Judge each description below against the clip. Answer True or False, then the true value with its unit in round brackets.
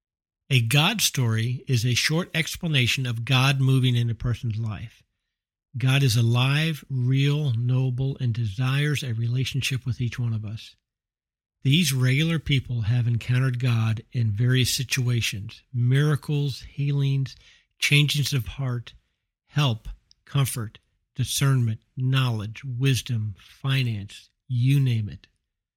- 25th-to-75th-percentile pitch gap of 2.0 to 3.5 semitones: True (2.7 semitones)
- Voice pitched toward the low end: True (125 Hz)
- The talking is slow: True (120 wpm)